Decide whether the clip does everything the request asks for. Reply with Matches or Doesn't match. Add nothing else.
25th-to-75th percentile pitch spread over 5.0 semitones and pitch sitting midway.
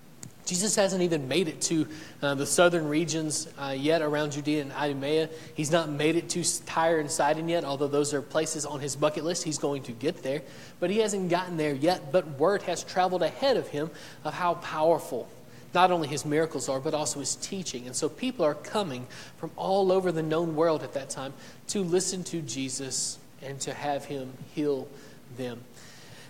Doesn't match